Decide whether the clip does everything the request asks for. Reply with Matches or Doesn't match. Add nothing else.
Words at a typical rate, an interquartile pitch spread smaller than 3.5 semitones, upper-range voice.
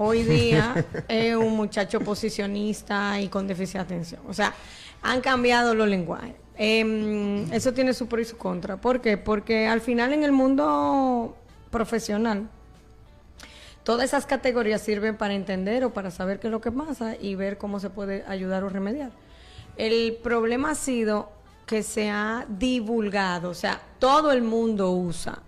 Matches